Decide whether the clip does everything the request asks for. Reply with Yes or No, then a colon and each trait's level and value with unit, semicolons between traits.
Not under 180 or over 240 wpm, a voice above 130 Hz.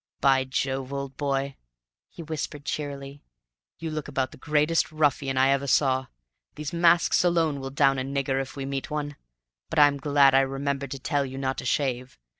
Yes: average, 185 wpm; medium, 140 Hz